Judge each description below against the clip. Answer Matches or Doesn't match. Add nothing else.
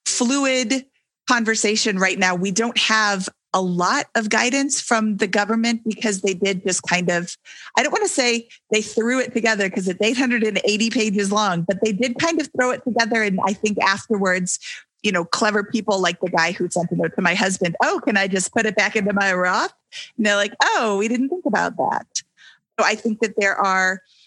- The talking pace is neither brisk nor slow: Doesn't match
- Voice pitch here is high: Matches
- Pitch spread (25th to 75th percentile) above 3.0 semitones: Matches